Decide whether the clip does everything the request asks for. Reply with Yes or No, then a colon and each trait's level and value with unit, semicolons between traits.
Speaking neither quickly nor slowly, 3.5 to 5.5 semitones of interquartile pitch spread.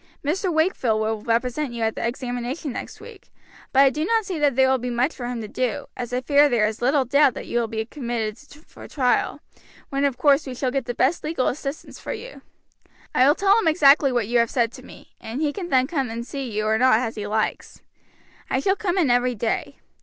No: fast, 240 wpm; average, 3.9 semitones